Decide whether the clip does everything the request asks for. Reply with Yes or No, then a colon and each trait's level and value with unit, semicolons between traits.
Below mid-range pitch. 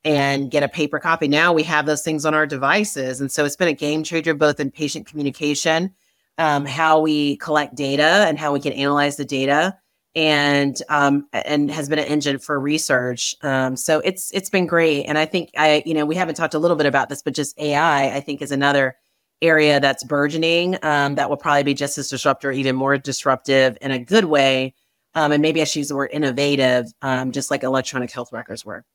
No: medium, 145 Hz